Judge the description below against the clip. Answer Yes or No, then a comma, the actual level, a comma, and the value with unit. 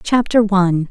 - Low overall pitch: No, high, 200 Hz